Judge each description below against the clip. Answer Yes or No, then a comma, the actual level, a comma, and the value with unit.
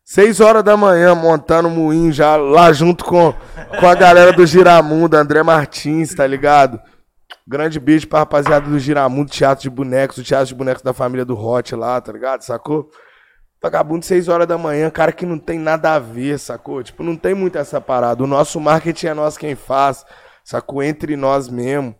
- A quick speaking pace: Yes, fast, 195 wpm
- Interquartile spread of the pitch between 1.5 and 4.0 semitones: Yes, average, 3.4 semitones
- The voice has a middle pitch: Yes, medium, 150 Hz